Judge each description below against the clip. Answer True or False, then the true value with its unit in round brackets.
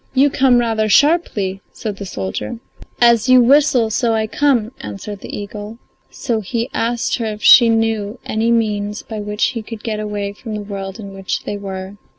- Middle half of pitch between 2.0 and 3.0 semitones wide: True (2.5 semitones)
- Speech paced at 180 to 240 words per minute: True (185 wpm)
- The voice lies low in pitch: False (220 Hz)